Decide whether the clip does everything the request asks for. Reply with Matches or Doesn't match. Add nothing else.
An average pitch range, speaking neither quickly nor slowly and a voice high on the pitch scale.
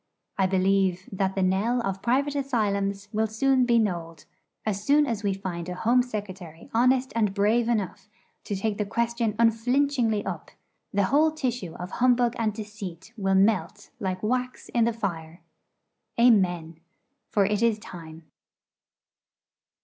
Matches